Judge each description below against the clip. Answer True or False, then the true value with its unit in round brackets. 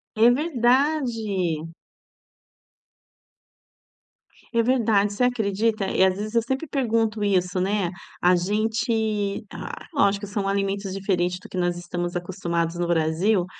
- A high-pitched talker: True (200 Hz)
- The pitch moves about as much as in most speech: True (4.0 semitones)